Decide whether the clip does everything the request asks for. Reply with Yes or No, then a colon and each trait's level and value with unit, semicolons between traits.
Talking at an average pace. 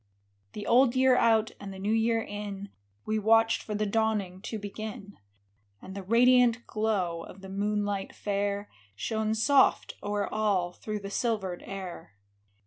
Yes: average, 150 wpm